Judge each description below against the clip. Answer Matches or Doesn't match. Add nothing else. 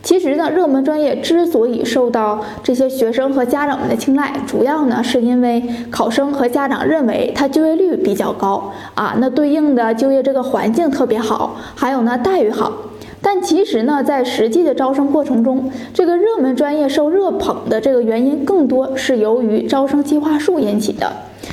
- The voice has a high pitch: Matches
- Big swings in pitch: Doesn't match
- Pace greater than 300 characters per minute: Doesn't match